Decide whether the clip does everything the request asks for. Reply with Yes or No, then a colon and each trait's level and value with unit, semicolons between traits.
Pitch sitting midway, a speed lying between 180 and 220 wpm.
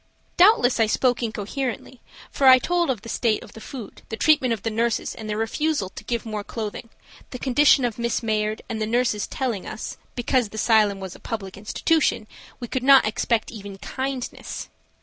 No: high, 230 Hz; average, 190 wpm